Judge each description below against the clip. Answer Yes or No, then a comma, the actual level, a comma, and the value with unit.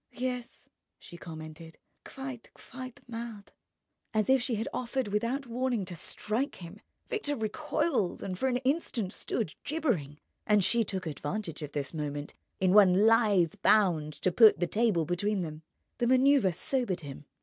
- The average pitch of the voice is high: Yes, high, 210 Hz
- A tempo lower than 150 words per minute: No, average, 155 wpm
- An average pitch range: No, wide, 6.3 semitones